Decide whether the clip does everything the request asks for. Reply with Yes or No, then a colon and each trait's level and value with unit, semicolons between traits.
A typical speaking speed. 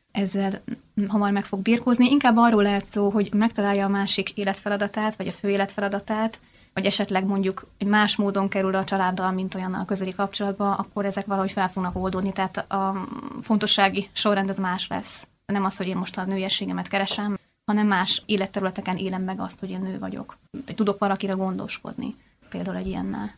No: fast, 175 wpm